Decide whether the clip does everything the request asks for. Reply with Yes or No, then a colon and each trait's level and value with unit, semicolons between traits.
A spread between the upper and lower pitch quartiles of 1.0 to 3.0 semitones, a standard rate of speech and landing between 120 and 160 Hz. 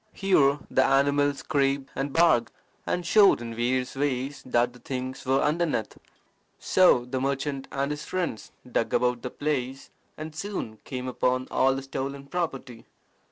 Yes: narrow, 2.6 semitones; average, 155 wpm; low, 135 Hz